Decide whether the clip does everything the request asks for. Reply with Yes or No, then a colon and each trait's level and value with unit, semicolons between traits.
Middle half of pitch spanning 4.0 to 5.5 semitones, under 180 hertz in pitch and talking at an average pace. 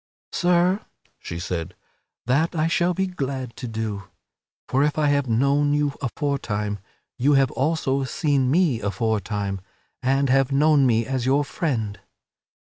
Yes: average, 4.5 semitones; low, 135 Hz; average, 145 wpm